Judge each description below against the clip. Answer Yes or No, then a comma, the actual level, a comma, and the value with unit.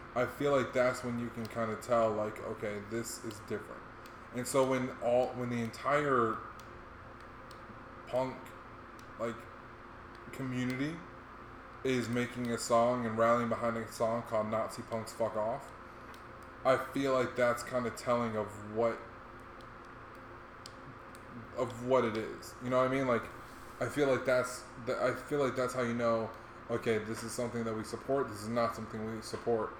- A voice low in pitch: Yes, low, 115 Hz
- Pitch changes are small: Yes, narrow, 2.0 semitones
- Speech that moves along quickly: No, average, 165 wpm